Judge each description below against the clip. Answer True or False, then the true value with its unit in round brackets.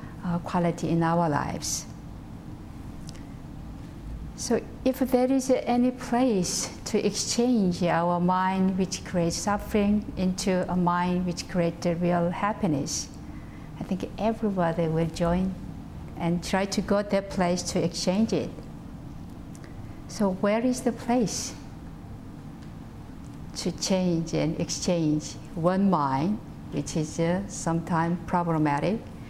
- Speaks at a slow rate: True (115 wpm)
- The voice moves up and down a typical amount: True (3.4 semitones)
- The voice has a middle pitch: True (180 Hz)